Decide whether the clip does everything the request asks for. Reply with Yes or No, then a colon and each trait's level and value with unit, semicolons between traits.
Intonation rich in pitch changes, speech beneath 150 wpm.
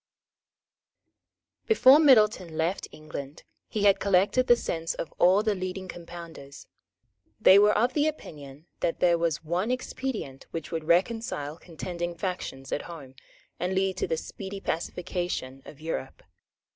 No: average, 4.0 semitones; slow, 135 wpm